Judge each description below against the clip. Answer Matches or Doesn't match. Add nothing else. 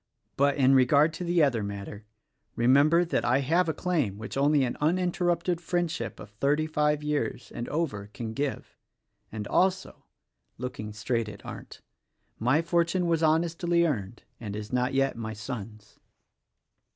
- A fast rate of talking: Doesn't match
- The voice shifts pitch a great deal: Matches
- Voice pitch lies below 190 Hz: Matches